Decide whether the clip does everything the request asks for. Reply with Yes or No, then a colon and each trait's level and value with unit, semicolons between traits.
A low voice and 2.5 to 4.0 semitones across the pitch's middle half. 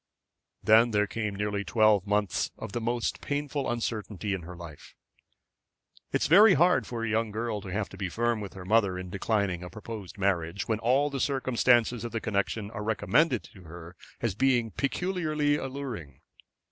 Yes: low, 110 Hz; average, 3.7 semitones